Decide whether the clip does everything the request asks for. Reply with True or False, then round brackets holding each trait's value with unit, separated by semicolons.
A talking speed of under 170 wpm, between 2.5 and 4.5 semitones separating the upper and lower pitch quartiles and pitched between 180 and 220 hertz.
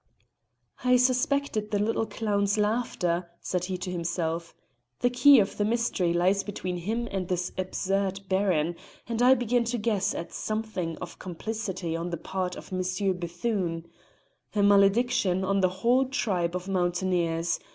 True (150 wpm; 3.8 semitones; 190 Hz)